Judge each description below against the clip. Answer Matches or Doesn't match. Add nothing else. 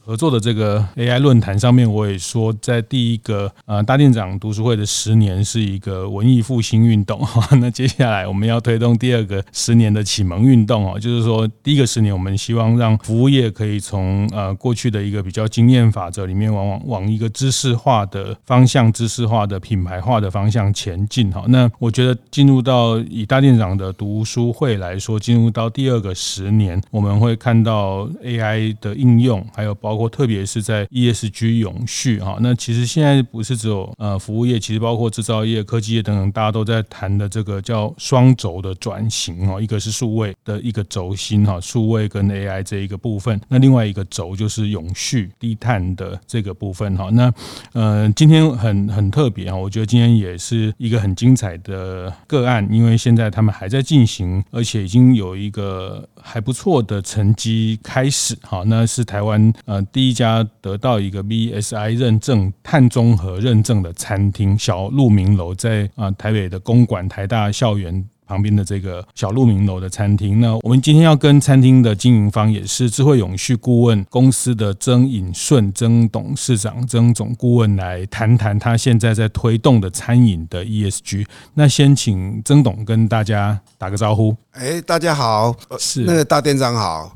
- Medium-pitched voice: Doesn't match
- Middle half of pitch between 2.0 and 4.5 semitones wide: Matches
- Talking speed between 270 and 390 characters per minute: Matches